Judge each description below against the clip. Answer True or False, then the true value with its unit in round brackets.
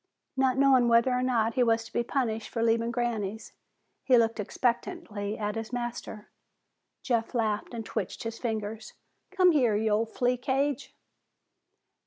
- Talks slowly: False (155 wpm)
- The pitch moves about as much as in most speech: False (2.3 semitones)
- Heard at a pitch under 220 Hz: False (230 Hz)